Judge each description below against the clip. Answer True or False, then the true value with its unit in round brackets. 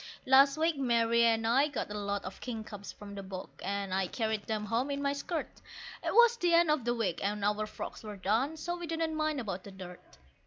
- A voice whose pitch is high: True (230 Hz)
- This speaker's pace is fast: True (230 wpm)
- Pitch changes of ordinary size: False (6.0 semitones)